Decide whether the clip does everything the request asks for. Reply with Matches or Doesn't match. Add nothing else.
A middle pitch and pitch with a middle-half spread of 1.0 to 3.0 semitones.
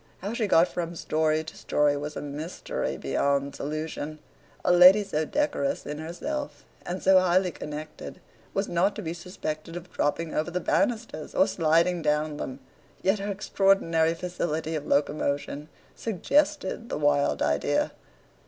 Doesn't match